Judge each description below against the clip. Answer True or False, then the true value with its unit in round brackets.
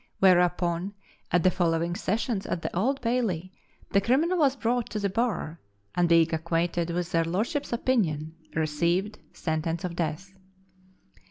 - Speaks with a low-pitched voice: False (180 Hz)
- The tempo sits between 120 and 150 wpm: True (145 wpm)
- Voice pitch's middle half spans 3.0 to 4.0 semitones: False (5.0 semitones)